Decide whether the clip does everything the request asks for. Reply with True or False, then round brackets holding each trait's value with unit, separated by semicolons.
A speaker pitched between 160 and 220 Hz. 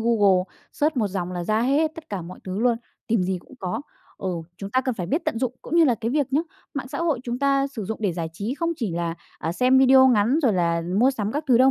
False (235 Hz)